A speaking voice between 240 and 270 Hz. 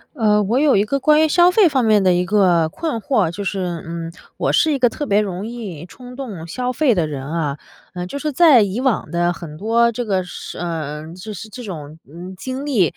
No: high, 205 Hz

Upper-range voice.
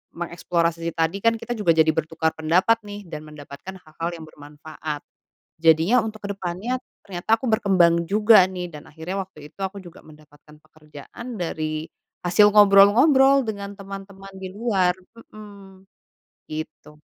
No: medium, 180 Hz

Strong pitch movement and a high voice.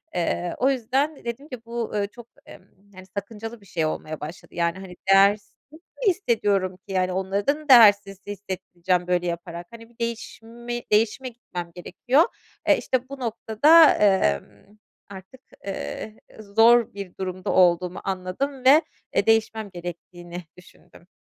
No: average, 4.6 semitones; high, 205 Hz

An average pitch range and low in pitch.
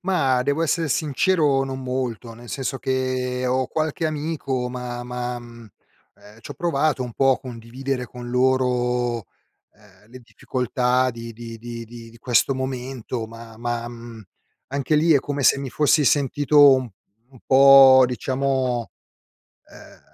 No: narrow, 2.3 semitones; low, 125 Hz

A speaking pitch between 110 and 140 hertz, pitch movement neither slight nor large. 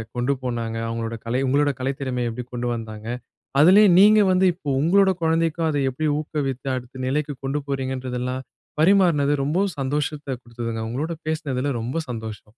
Yes: low, 135 Hz; average, 4.2 semitones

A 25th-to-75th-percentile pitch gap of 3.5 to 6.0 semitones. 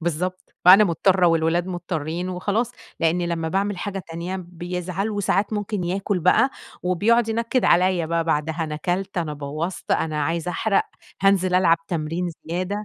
No: average, 2.8 semitones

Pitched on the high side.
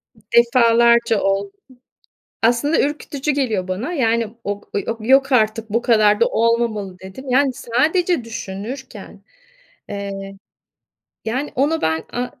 Yes: high, 230 Hz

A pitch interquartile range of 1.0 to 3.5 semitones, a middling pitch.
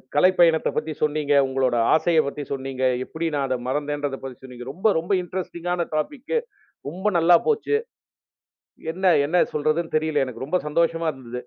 No: average, 4.1 semitones; medium, 155 Hz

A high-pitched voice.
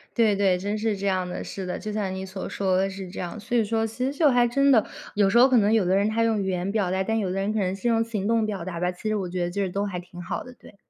Yes: high, 200 Hz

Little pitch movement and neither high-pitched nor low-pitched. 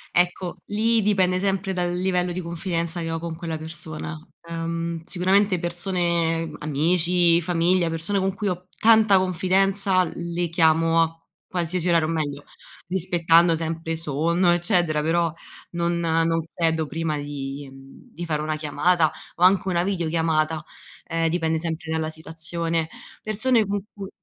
Yes: narrow, 2.1 semitones; medium, 170 Hz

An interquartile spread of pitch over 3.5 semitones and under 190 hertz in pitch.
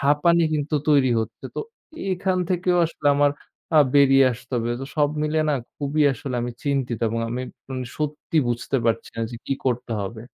Yes: average, 3.9 semitones; medium, 140 Hz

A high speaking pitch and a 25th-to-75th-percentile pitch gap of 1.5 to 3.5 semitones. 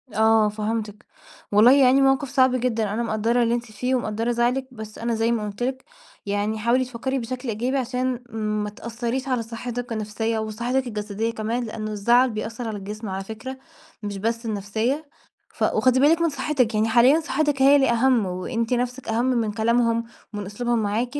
Yes: high, 235 Hz; average, 2.8 semitones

